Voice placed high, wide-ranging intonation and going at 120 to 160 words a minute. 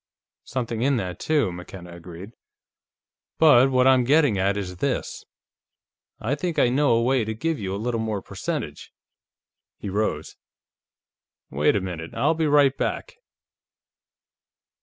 No: low, 115 Hz; wide, 6.1 semitones; average, 140 wpm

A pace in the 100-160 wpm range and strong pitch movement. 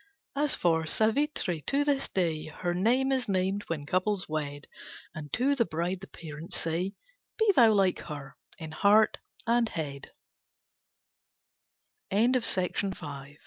Yes: slow, 135 wpm; wide, 6.4 semitones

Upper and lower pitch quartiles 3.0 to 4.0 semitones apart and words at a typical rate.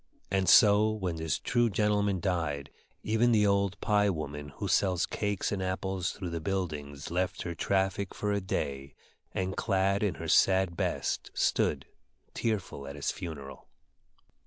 Yes: average, 3.5 semitones; average, 155 wpm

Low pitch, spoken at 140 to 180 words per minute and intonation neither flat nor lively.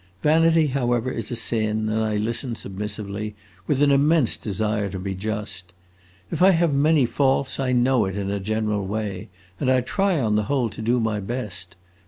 No: low, 110 Hz; average, 190 wpm; average, 4.2 semitones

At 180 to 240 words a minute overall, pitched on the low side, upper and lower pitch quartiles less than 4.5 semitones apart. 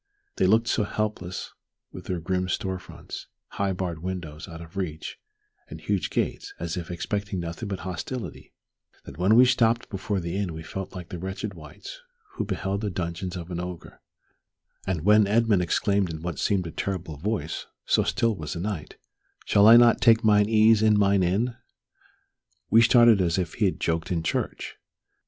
Yes: average, 185 wpm; very low, 95 Hz; average, 3.7 semitones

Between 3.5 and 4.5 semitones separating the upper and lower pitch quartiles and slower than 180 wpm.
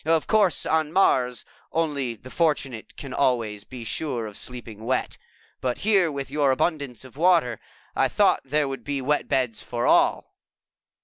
Yes: average, 4.0 semitones; average, 165 wpm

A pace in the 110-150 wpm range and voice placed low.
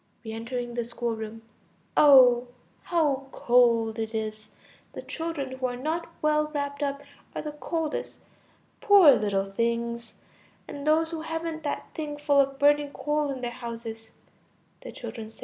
No: average, 145 wpm; very high, 265 Hz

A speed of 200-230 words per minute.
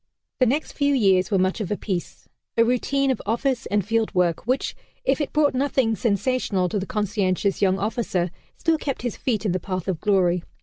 Yes: fast, 205 wpm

